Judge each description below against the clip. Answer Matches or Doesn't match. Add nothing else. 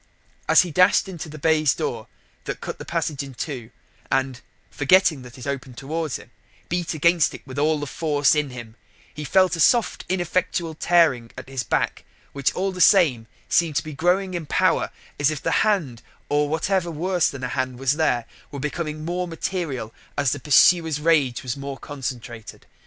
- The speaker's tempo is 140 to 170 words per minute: Doesn't match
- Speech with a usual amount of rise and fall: Matches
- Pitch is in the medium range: Matches